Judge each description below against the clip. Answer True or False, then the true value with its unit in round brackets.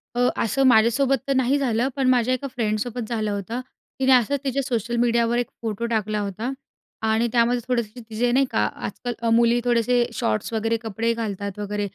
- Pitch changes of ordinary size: False (2.2 semitones)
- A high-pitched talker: True (235 Hz)